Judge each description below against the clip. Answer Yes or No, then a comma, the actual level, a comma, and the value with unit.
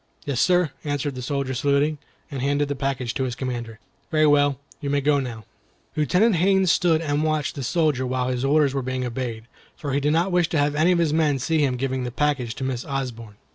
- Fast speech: Yes, fast, 225 wpm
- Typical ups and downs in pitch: Yes, average, 3.1 semitones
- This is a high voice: No, medium, 140 Hz